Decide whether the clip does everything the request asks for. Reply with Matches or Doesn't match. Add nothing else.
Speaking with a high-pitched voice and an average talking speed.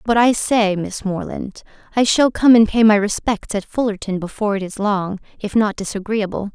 Matches